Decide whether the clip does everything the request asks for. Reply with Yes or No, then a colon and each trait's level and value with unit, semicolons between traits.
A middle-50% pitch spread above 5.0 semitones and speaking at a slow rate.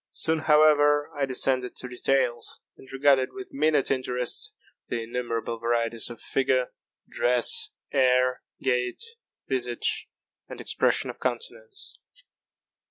No: average, 3.0 semitones; slow, 110 wpm